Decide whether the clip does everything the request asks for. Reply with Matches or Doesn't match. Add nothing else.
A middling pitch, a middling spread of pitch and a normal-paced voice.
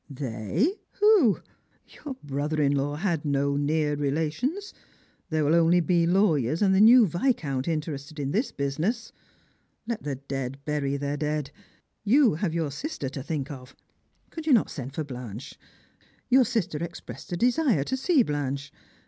Doesn't match